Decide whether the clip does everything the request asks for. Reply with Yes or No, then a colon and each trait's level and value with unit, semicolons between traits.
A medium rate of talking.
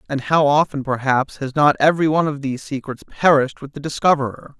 Yes: average, 195 wpm